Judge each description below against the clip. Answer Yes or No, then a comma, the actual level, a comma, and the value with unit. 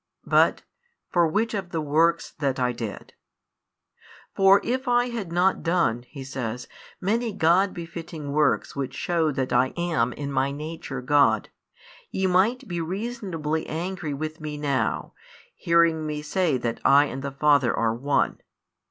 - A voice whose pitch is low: No, medium, 155 Hz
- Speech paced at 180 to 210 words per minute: No, average, 155 wpm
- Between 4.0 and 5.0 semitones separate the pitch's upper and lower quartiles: Yes, average, 4.5 semitones